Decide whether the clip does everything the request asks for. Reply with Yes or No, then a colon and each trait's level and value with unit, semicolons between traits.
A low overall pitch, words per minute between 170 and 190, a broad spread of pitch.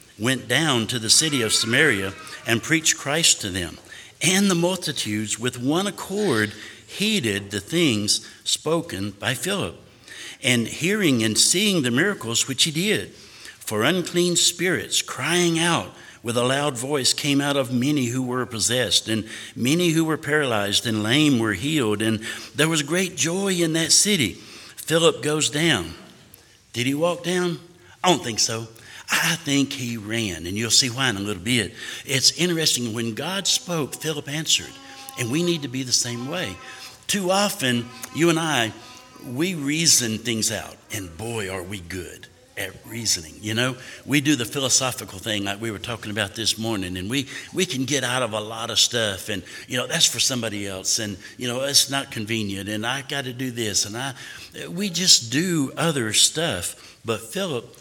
Yes: low, 130 Hz; average, 180 wpm; wide, 6.2 semitones